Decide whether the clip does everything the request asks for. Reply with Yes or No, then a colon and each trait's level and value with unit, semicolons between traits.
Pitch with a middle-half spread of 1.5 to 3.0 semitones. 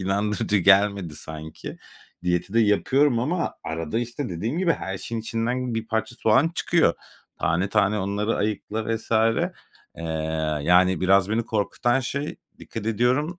No: average, 3.8 semitones